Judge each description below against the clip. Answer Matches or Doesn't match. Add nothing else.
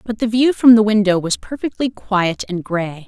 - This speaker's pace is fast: Matches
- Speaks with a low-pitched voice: Doesn't match